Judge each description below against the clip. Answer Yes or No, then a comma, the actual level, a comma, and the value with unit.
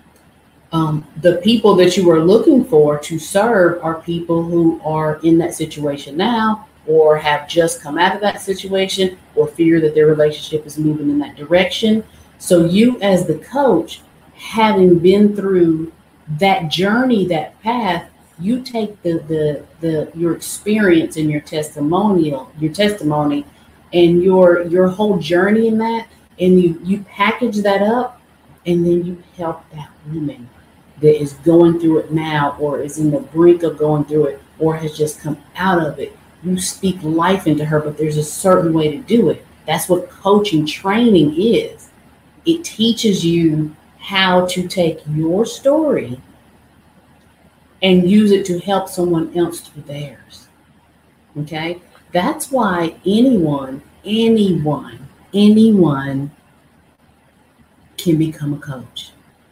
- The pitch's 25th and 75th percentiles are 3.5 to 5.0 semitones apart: Yes, average, 4.2 semitones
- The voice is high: No, medium, 170 Hz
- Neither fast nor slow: Yes, average, 145 wpm